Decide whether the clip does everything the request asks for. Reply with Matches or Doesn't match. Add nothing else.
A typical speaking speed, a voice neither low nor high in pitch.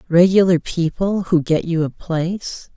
Matches